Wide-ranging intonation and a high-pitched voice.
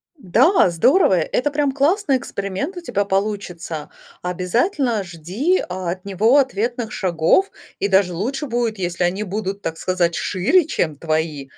Yes: wide, 6.8 semitones; high, 200 Hz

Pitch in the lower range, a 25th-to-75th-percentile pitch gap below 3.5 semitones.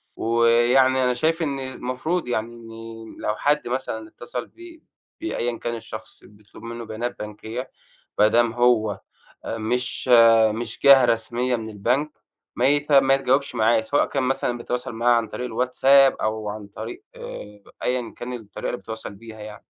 Yes: low, 120 Hz; average, 2.7 semitones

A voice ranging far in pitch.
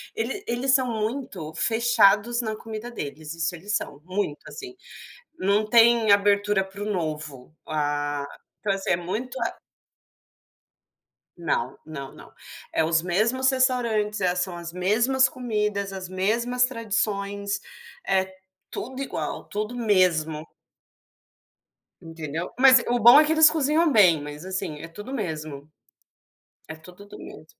Yes: wide, 6.1 semitones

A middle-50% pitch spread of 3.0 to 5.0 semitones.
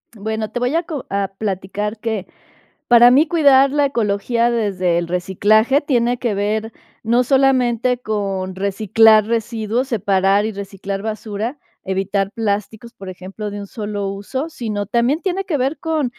Yes: average, 3.7 semitones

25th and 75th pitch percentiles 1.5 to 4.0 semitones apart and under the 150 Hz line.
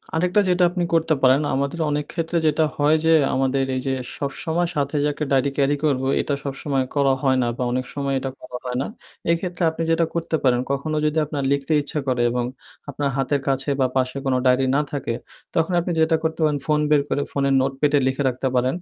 Yes: average, 3.1 semitones; medium, 140 Hz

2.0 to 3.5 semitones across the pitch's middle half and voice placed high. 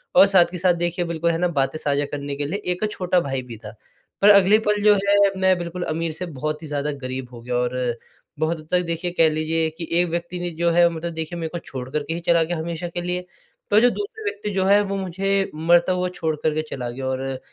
No: average, 3.2 semitones; medium, 170 Hz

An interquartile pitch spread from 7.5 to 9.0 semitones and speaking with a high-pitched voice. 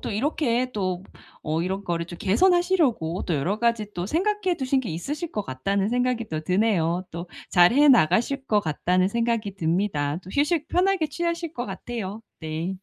Yes: wide, 7.8 semitones; high, 210 Hz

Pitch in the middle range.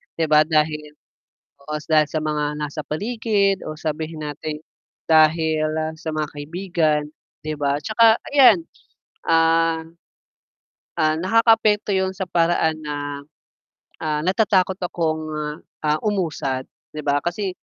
Yes: medium, 160 Hz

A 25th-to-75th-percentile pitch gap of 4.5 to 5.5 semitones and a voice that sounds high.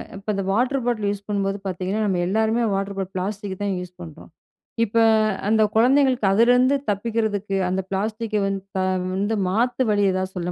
No: average, 2.8 semitones; high, 205 Hz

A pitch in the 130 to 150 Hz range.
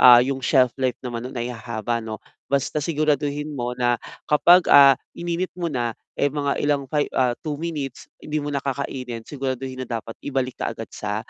Yes: low, 135 Hz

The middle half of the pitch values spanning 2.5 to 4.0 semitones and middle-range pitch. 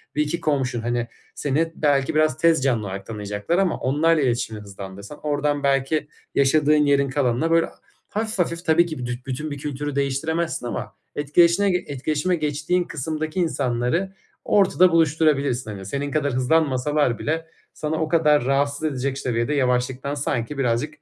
Yes: average, 3.7 semitones; medium, 145 Hz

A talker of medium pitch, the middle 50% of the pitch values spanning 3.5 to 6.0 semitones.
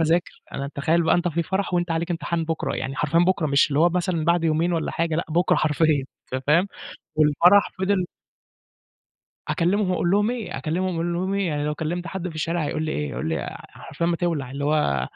No: medium, 165 Hz; narrow, 2.6 semitones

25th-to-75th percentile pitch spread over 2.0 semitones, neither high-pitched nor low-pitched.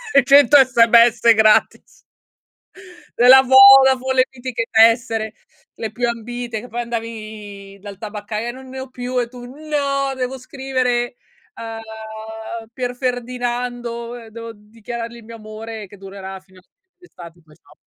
No: average, 2.7 semitones; high, 235 Hz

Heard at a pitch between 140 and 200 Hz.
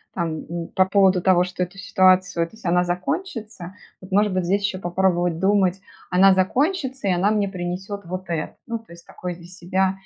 Yes: medium, 185 Hz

